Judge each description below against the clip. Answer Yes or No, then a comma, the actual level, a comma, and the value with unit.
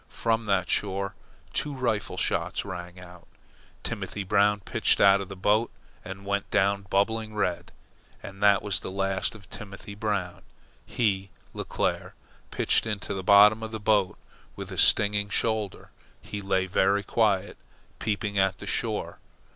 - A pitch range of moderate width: No, narrow, 1.5 semitones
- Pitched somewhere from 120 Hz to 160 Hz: No, low, 100 Hz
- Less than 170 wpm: Yes, average, 150 wpm